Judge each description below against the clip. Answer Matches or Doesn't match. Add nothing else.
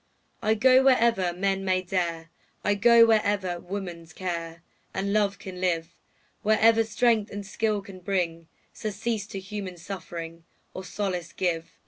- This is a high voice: Matches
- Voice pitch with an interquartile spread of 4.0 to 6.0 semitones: Doesn't match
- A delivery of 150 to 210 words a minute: Doesn't match